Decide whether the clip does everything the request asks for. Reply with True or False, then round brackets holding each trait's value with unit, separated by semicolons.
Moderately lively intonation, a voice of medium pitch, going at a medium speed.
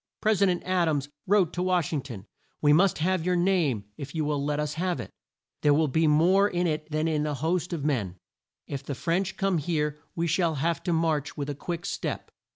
False (3.3 semitones; 160 Hz; 230 wpm)